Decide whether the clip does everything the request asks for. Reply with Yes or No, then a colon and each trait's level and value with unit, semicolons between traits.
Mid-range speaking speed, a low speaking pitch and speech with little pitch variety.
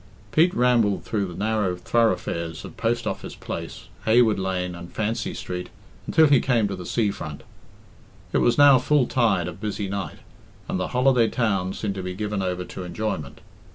No: average, 180 wpm; low, 105 Hz; average, 4.4 semitones